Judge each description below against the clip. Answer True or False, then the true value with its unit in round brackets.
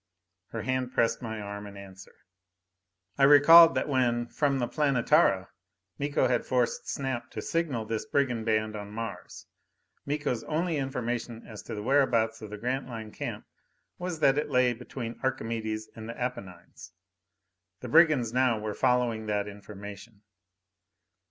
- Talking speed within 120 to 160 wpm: True (145 wpm)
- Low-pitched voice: True (120 Hz)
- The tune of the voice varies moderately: True (3.6 semitones)